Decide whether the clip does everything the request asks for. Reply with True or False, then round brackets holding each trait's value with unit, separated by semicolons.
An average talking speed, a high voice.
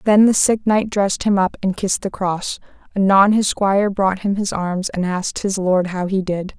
False (230 wpm; 195 Hz)